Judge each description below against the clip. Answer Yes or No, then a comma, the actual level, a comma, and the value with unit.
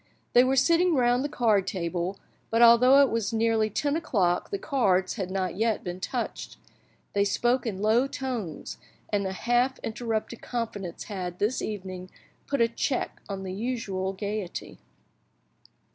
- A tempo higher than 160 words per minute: No, average, 155 wpm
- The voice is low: No, high, 220 Hz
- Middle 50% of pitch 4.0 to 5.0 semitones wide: Yes, average, 4.5 semitones